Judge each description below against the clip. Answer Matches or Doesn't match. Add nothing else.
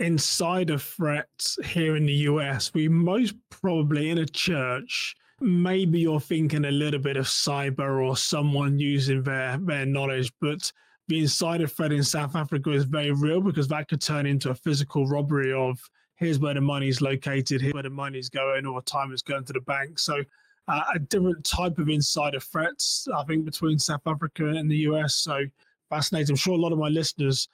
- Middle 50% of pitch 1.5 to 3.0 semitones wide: Matches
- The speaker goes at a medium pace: Matches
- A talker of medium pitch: Matches